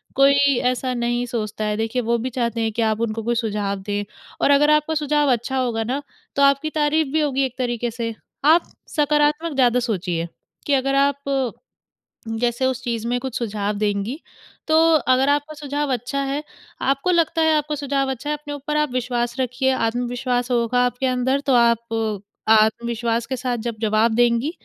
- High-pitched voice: Yes, very high, 250 Hz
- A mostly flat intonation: No, average, 3.4 semitones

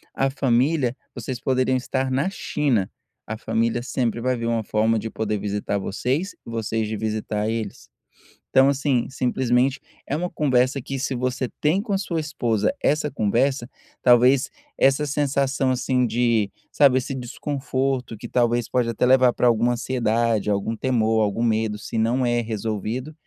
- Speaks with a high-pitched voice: No, low, 125 Hz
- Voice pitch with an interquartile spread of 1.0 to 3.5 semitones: Yes, average, 3.0 semitones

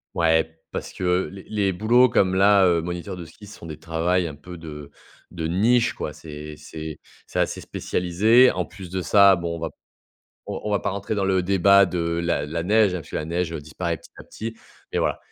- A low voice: Yes, very low, 90 Hz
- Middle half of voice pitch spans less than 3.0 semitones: No, average, 3.3 semitones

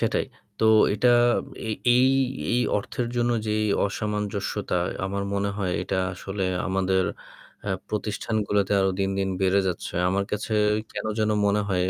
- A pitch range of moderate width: No, narrow, 1.7 semitones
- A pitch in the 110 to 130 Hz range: No, low, 100 Hz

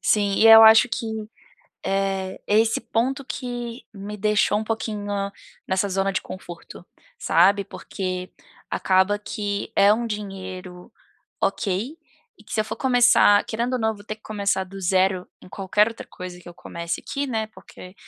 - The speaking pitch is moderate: No, high, 205 Hz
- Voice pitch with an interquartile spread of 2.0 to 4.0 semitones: Yes, average, 2.9 semitones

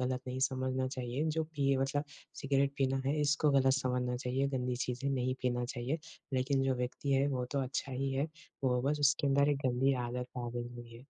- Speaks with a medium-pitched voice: No, low, 130 Hz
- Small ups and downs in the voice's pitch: Yes, narrow, 1.7 semitones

